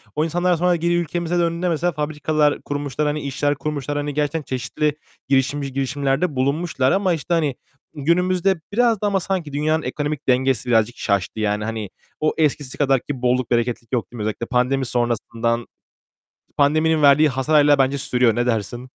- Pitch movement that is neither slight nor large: Yes, average, 3.9 semitones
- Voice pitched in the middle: Yes, medium, 145 Hz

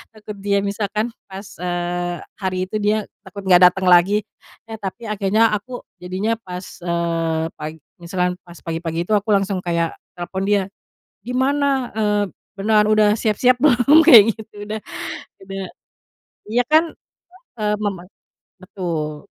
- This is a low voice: No, high, 200 Hz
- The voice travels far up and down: No, average, 3.3 semitones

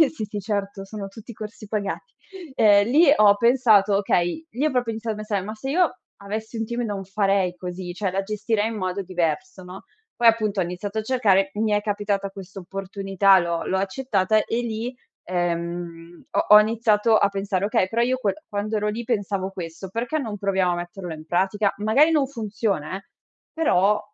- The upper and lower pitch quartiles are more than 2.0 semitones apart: Yes, average, 2.7 semitones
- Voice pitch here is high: Yes, high, 205 Hz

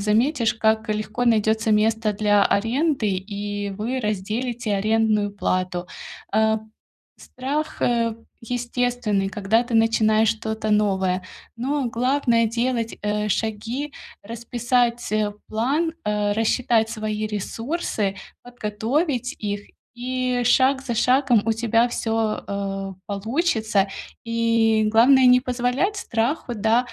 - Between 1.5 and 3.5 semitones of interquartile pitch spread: Yes, average, 2.7 semitones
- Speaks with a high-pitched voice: Yes, high, 225 Hz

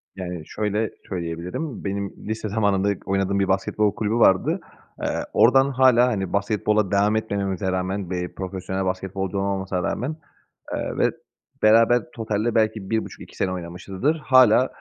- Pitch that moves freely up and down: No, average, 2.7 semitones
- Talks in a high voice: No, low, 100 Hz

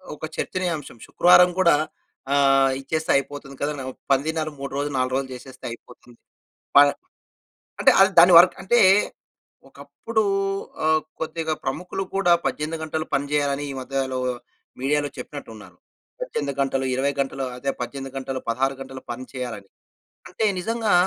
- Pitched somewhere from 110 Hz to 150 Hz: Yes, medium, 140 Hz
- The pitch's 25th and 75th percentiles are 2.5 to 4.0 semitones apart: Yes, average, 3.2 semitones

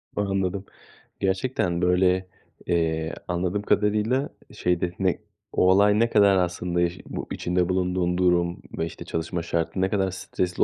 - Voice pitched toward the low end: Yes, very low, 90 Hz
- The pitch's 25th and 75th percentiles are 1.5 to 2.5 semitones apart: Yes, narrow, 1.8 semitones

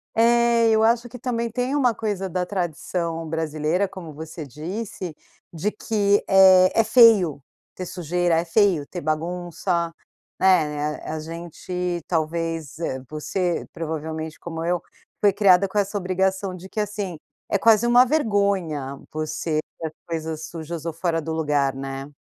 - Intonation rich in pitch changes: No, average, 4.1 semitones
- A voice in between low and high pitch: Yes, medium, 175 Hz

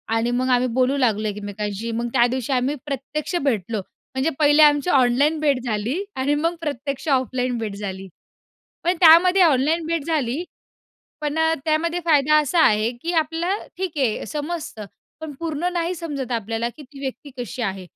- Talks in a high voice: Yes, very high, 275 Hz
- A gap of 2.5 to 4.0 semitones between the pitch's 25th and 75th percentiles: No, average, 5.1 semitones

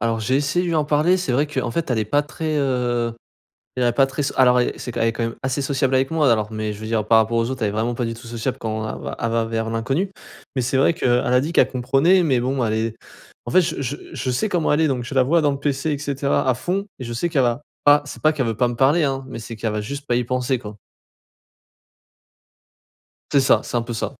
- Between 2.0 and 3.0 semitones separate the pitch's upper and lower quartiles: No, average, 3.8 semitones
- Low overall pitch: Yes, low, 130 Hz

